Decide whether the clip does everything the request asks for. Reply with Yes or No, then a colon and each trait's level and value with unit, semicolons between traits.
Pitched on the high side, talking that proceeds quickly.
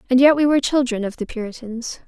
Yes: very high, 250 Hz; fast, 230 wpm